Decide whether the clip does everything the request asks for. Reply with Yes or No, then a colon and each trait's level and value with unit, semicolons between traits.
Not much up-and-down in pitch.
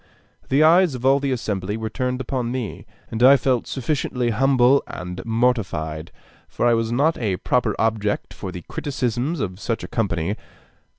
No: average, 4.0 semitones